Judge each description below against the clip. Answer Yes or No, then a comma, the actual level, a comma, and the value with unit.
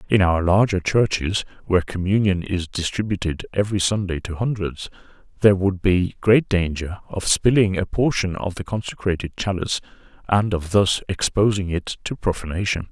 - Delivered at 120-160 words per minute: Yes, average, 150 wpm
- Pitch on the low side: Yes, very low, 95 Hz